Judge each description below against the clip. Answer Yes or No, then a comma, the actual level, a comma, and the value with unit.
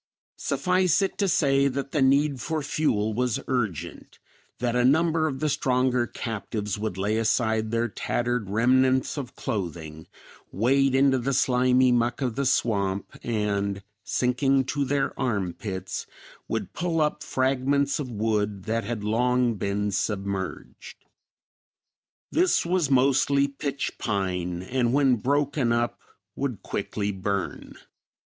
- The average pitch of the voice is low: Yes, low, 125 Hz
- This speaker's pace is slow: Yes, slow, 130 wpm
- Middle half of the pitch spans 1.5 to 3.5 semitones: No, average, 4.7 semitones